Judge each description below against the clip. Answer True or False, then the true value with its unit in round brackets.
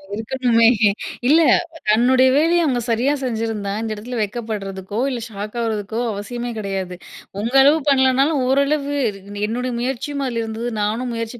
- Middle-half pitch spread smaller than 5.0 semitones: True (3.4 semitones)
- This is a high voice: True (235 Hz)